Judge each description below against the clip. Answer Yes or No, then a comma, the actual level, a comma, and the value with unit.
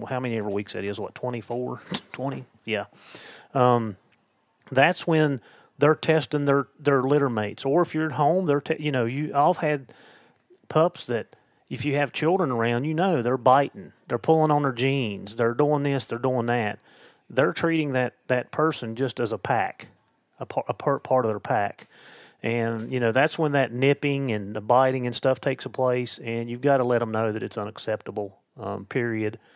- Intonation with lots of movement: No, average, 3.7 semitones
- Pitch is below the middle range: Yes, low, 130 Hz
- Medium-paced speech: Yes, average, 195 wpm